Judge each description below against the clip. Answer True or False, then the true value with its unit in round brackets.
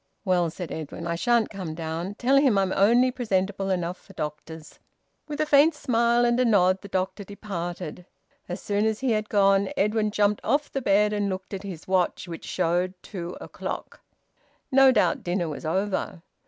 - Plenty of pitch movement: False (3.8 semitones)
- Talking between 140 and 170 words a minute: False (180 wpm)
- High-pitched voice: True (195 Hz)